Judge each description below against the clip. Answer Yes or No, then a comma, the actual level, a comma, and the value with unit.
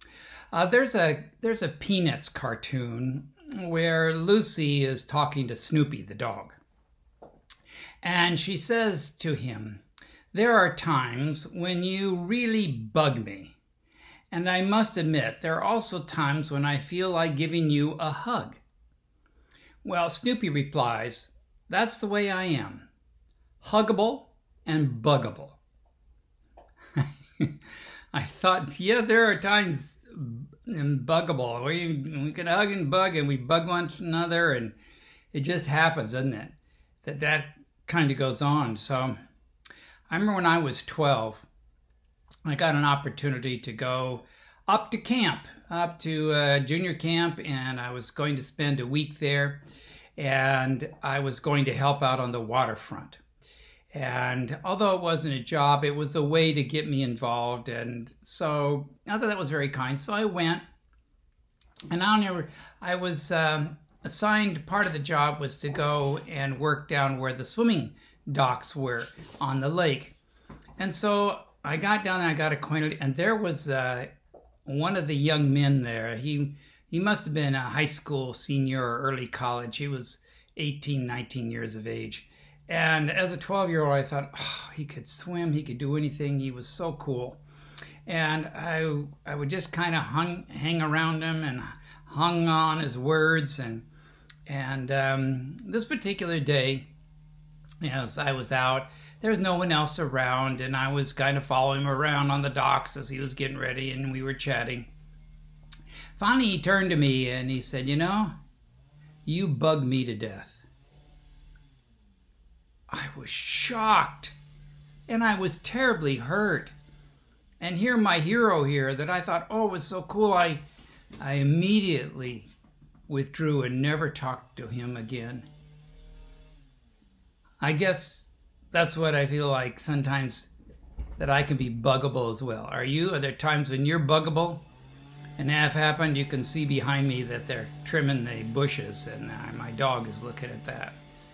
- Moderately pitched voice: Yes, medium, 145 Hz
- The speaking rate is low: No, average, 160 wpm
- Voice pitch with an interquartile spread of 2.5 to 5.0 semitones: Yes, average, 4.0 semitones